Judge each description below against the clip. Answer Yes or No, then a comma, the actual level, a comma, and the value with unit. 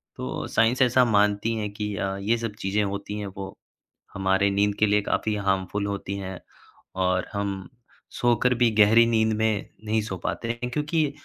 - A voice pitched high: No, low, 105 Hz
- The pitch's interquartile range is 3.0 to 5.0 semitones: No, narrow, 2.4 semitones